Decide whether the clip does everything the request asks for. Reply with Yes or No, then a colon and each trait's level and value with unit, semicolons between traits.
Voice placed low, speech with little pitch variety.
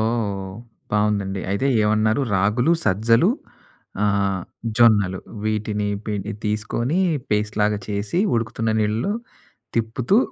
Yes: low, 105 Hz; narrow, 1.9 semitones